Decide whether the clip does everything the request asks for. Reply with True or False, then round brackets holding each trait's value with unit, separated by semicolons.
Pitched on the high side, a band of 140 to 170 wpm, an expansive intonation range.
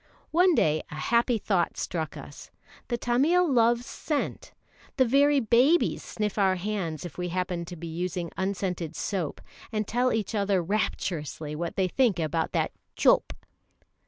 True (200 Hz; 155 wpm; 5.9 semitones)